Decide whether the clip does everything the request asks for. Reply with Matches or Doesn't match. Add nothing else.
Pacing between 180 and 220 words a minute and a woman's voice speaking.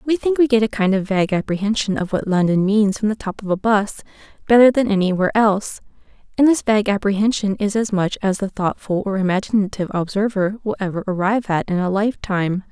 Matches